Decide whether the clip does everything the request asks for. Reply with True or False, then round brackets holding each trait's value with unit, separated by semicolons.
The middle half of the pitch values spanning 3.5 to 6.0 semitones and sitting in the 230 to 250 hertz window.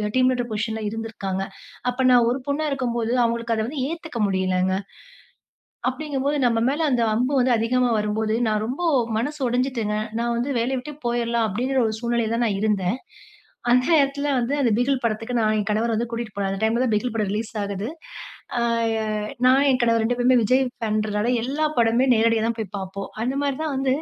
False (3.0 semitones; 235 Hz)